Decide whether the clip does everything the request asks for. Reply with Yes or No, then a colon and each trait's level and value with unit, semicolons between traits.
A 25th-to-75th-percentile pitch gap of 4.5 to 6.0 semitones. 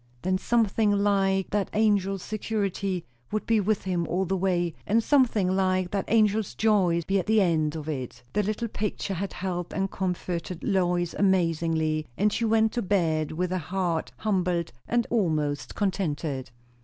No: average, 3.2 semitones